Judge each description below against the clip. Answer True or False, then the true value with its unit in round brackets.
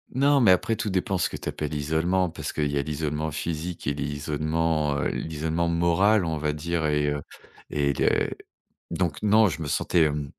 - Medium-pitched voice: False (80 Hz)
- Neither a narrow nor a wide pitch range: True (3.0 semitones)